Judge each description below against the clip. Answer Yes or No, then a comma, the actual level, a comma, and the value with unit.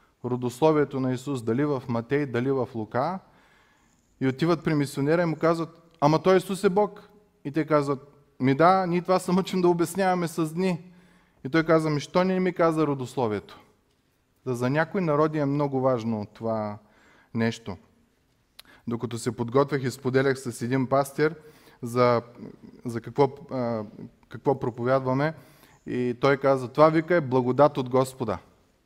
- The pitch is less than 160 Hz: Yes, medium, 140 Hz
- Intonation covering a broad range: No, average, 4.6 semitones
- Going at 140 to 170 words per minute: Yes, average, 155 wpm